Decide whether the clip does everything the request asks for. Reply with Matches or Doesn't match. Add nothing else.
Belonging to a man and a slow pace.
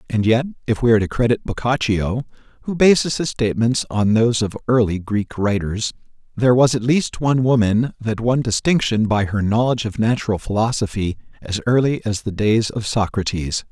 Doesn't match